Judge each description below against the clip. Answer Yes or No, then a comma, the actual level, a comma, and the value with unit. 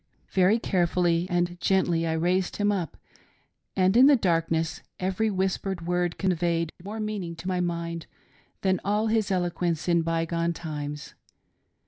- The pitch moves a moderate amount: No, narrow, 2.3 semitones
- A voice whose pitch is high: No, medium, 175 Hz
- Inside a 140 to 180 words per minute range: Yes, average, 150 wpm